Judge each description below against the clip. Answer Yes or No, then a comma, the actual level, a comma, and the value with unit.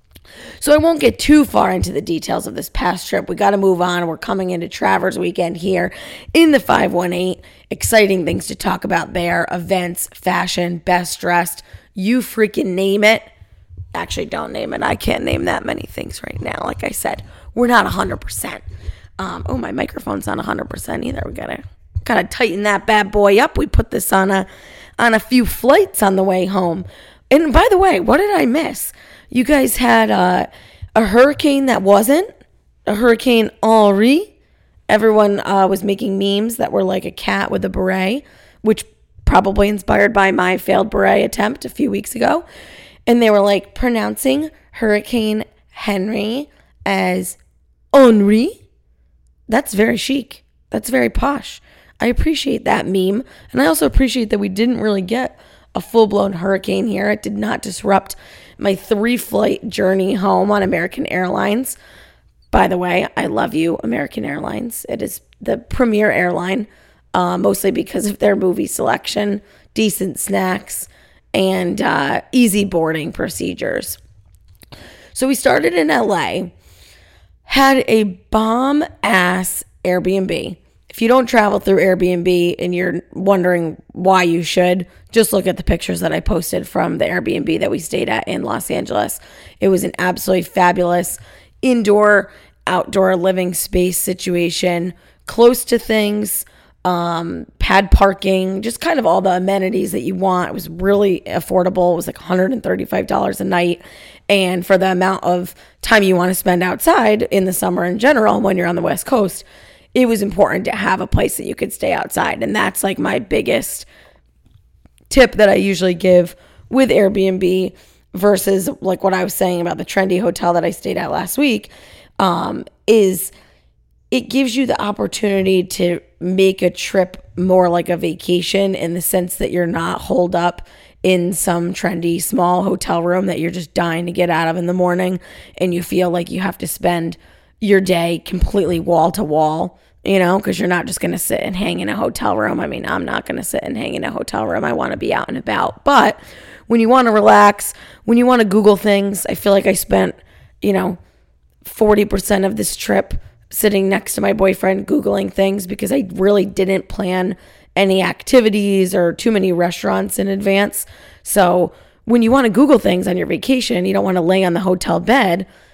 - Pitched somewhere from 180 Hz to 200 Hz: Yes, high, 190 Hz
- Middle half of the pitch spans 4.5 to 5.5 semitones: No, average, 3.5 semitones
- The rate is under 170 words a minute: No, average, 180 wpm